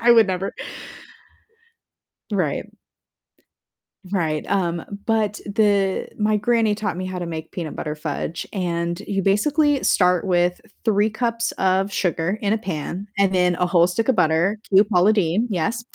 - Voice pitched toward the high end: Yes, high, 195 Hz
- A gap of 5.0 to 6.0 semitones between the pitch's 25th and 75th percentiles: No, average, 3.4 semitones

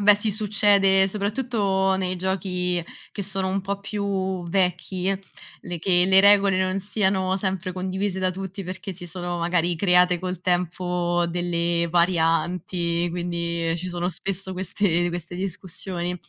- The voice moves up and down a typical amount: No, narrow, 1.7 semitones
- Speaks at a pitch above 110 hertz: Yes, medium, 185 Hz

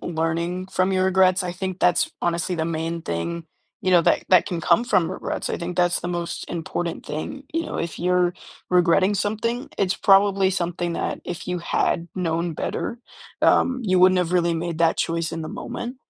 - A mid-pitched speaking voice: Yes, medium, 175 Hz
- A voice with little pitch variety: Yes, narrow, 2.0 semitones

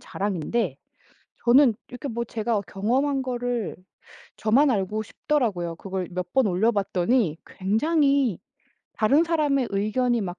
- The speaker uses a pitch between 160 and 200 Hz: No, high, 230 Hz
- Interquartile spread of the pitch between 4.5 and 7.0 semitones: Yes, average, 5.2 semitones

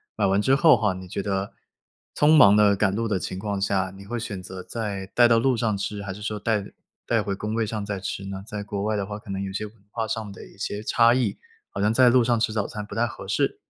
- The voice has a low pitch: Yes, low, 105 Hz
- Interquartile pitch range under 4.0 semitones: Yes, narrow, 2.4 semitones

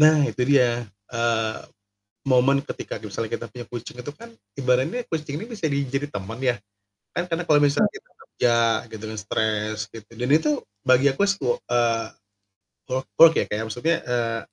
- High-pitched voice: No, low, 125 Hz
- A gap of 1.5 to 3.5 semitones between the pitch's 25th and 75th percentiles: No, average, 4.3 semitones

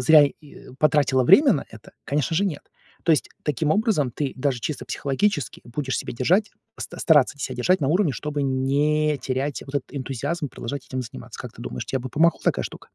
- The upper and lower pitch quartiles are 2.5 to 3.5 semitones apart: Yes, average, 2.9 semitones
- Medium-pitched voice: Yes, medium, 145 Hz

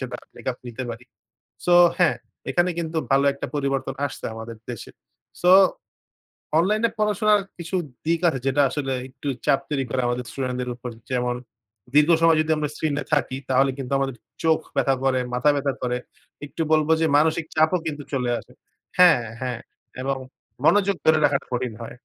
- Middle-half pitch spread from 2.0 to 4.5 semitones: Yes, average, 3.9 semitones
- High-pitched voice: No, medium, 140 Hz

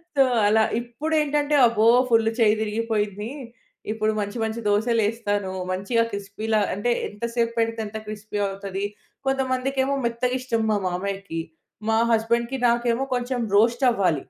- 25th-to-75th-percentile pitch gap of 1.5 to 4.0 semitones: Yes, narrow, 2.6 semitones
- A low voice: No, high, 225 Hz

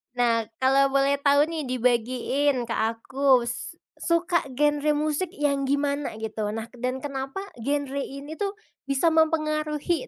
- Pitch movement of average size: Yes, average, 3.1 semitones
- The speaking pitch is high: Yes, very high, 280 Hz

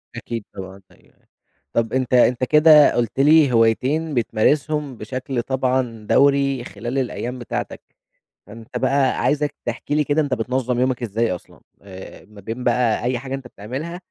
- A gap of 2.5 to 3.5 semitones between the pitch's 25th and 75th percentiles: Yes, average, 3.2 semitones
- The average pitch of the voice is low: Yes, low, 125 Hz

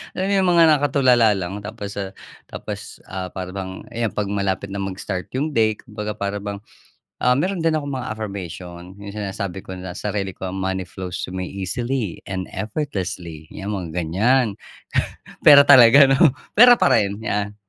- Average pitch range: Yes, average, 4.5 semitones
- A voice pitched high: No, low, 100 Hz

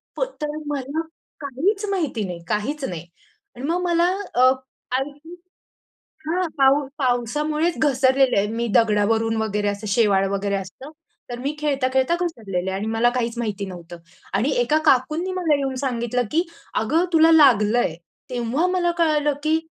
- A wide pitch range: Yes, wide, 5.7 semitones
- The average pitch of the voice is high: Yes, very high, 260 Hz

